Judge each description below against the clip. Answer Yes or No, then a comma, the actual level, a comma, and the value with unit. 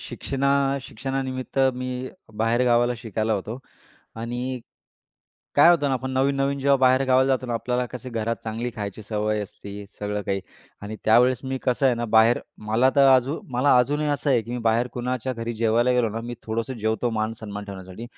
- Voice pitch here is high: No, low, 120 Hz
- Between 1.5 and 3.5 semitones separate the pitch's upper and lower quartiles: Yes, average, 2.8 semitones